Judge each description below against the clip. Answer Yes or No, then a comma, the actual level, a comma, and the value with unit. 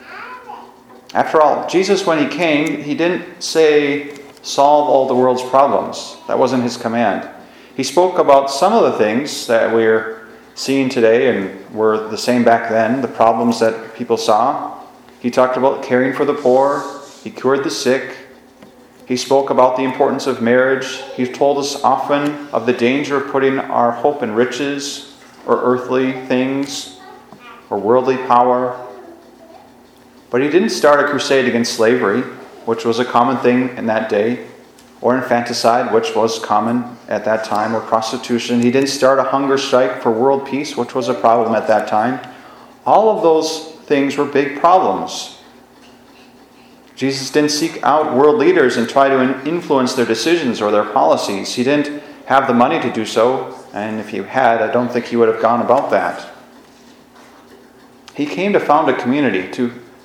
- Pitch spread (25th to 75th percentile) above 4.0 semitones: No, average, 2.9 semitones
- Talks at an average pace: Yes, average, 170 wpm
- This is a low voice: Yes, low, 130 Hz